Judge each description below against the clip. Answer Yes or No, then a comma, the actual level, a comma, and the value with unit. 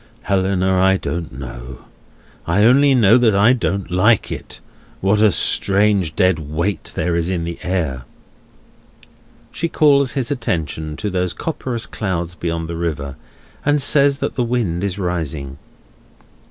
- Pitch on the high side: No, very low, 95 Hz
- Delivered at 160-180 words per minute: No, average, 145 wpm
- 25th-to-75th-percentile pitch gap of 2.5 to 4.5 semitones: No, wide, 5.6 semitones